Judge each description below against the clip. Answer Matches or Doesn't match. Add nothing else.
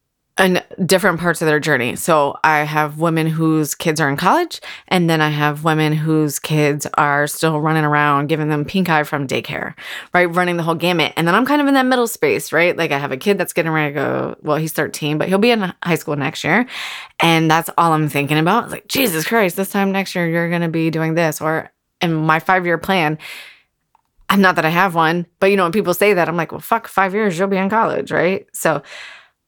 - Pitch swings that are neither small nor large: Matches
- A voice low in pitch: Doesn't match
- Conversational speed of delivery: Doesn't match